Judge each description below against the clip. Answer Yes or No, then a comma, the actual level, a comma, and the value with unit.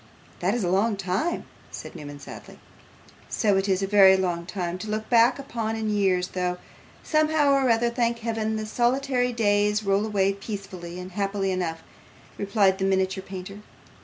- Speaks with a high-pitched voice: Yes, high, 200 Hz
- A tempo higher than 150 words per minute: Yes, average, 170 wpm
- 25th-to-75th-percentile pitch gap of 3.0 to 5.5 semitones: Yes, average, 3.3 semitones